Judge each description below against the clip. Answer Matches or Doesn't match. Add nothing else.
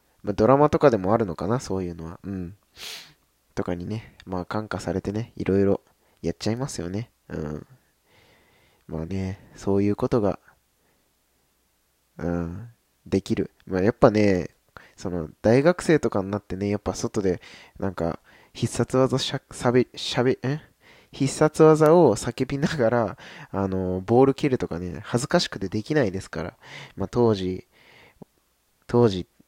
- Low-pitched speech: Matches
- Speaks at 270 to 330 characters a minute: Matches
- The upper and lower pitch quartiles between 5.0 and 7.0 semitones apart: Matches